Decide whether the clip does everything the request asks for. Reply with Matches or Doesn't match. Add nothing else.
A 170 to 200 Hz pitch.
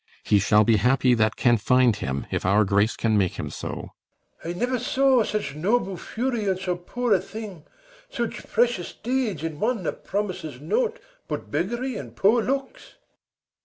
Matches